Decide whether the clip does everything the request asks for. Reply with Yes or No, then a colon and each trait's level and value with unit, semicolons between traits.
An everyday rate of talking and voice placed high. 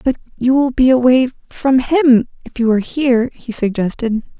Yes: average, 150 wpm; very high, 250 Hz